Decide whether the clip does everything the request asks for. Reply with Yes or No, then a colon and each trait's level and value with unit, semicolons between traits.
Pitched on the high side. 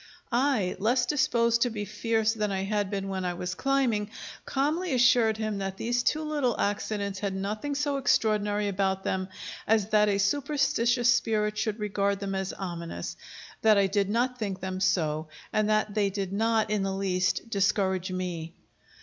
Yes: high, 210 Hz